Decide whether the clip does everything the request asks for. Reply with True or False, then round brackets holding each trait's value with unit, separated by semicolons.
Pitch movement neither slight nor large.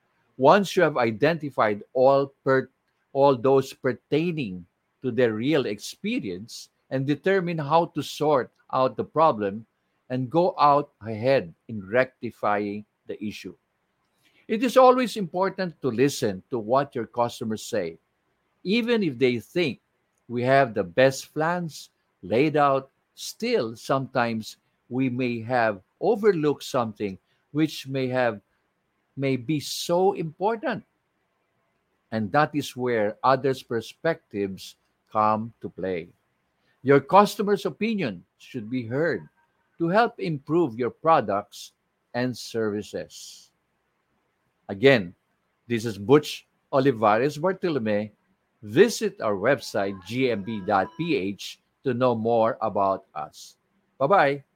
False (6.1 semitones)